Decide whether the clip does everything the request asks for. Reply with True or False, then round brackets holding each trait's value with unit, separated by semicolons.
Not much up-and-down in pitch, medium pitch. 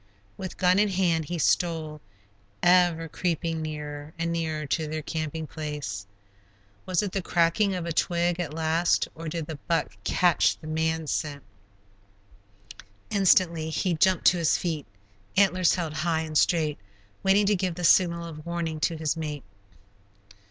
True (2.1 semitones; 165 Hz)